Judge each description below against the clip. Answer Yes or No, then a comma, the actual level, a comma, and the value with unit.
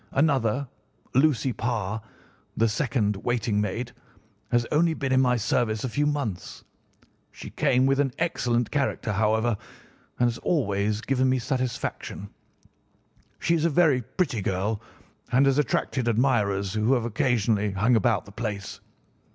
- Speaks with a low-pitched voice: Yes, low, 120 Hz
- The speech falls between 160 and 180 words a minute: No, average, 145 wpm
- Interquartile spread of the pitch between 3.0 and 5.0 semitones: Yes, average, 3.9 semitones